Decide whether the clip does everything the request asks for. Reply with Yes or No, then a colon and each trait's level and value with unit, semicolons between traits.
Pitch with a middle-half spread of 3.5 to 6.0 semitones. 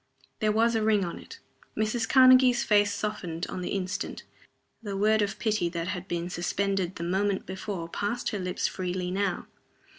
No: average, 3.0 semitones